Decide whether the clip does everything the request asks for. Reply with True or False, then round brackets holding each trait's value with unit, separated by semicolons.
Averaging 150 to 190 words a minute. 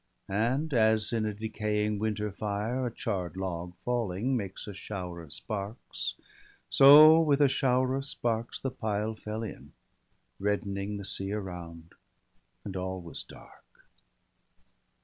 False (140 wpm)